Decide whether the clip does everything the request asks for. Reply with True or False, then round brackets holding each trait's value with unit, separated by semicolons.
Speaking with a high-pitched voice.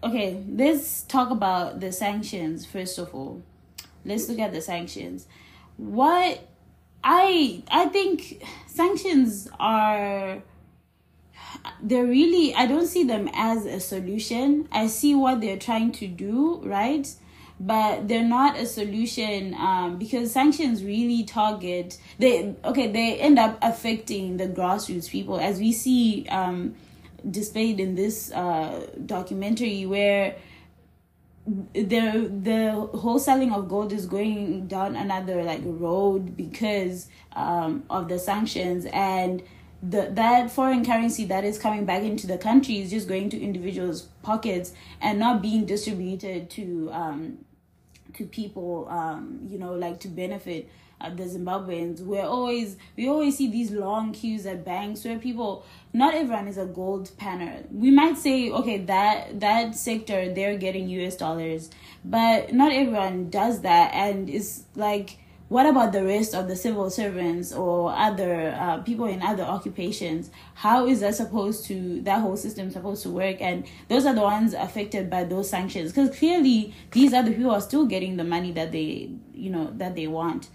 True (205 Hz)